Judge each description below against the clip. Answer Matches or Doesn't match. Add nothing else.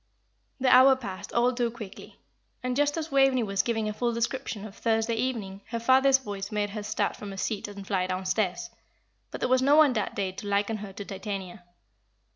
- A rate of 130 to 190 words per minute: Doesn't match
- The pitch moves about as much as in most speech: Matches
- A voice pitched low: Doesn't match